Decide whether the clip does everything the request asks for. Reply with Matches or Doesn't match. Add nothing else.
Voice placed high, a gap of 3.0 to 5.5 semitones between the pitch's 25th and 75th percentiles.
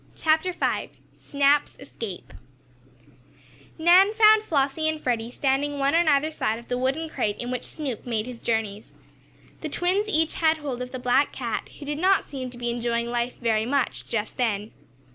Matches